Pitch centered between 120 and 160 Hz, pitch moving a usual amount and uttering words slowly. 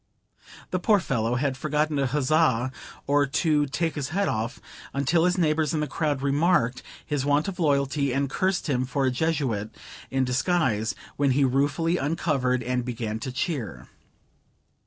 No: medium, 140 Hz; average, 3.7 semitones; average, 160 wpm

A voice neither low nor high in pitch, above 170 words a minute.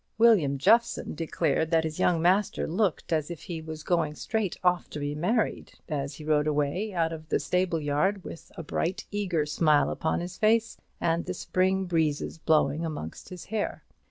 Yes: medium, 165 Hz; average, 185 wpm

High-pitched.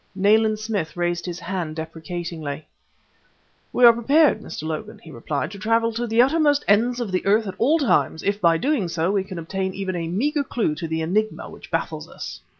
Yes: high, 195 Hz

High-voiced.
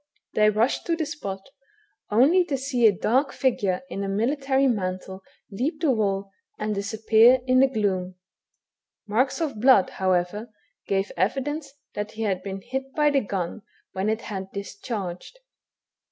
Yes: high, 220 Hz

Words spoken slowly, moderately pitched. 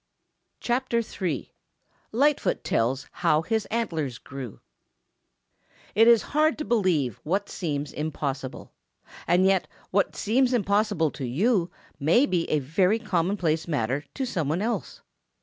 Yes: slow, 130 wpm; medium, 180 Hz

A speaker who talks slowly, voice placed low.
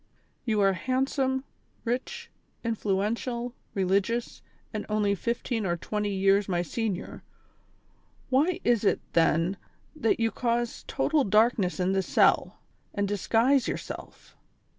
No: slow, 120 wpm; high, 220 Hz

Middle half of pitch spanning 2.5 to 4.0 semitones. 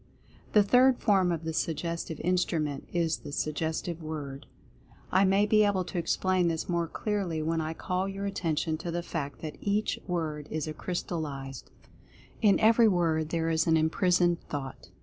Yes: average, 3.0 semitones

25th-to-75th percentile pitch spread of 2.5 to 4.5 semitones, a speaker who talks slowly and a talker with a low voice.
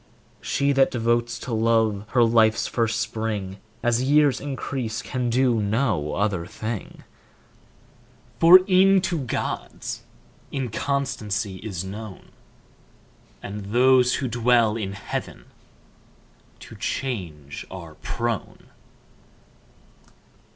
Yes: average, 3.9 semitones; slow, 100 wpm; low, 115 Hz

